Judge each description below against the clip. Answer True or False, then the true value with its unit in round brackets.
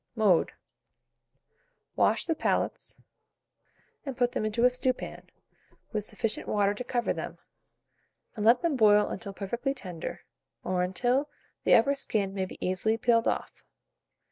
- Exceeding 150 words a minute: False (140 wpm)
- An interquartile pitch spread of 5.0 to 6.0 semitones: False (3.8 semitones)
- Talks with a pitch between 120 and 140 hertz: False (220 Hz)